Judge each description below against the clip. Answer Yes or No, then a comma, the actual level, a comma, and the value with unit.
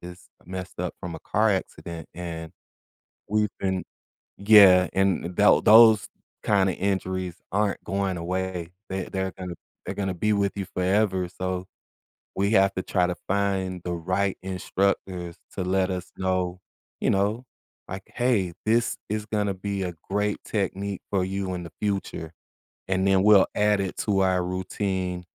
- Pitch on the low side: Yes, very low, 95 Hz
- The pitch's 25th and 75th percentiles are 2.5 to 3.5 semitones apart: No, narrow, 1.7 semitones